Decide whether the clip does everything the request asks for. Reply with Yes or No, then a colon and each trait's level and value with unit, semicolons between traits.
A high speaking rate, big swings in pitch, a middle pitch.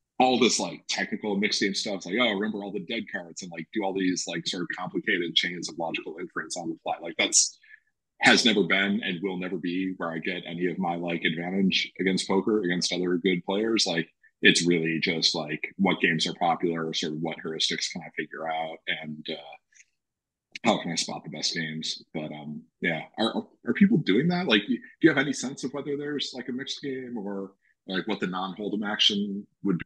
No: fast, 220 wpm; wide, 8.1 semitones; very low, 95 Hz